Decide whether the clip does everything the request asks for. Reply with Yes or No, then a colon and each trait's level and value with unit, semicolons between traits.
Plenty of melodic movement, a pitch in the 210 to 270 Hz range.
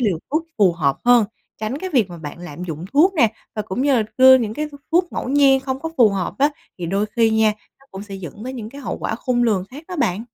Yes: wide, 5.7 semitones; high, 230 Hz